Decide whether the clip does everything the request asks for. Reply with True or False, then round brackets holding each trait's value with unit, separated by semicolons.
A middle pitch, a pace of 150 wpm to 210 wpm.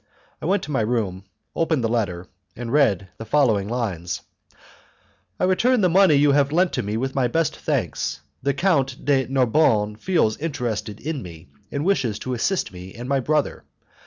False (130 Hz; 175 wpm)